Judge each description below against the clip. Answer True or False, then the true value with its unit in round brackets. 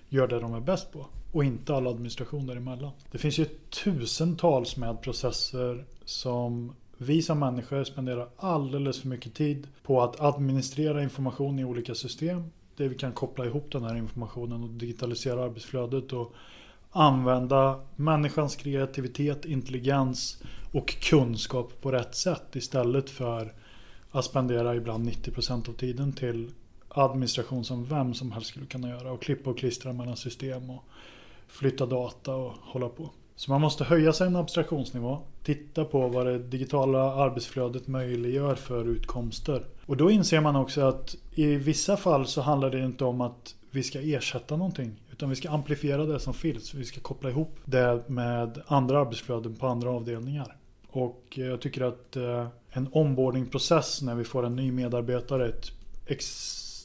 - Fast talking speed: False (160 wpm)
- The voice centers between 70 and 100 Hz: False (130 Hz)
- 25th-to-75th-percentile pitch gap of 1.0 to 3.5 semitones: True (2.7 semitones)